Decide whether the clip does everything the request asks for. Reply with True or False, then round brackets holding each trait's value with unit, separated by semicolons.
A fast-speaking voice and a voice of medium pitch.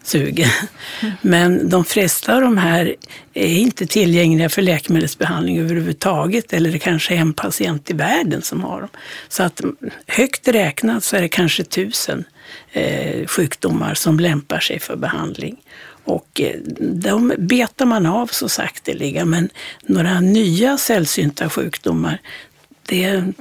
False (135 wpm; 180 Hz)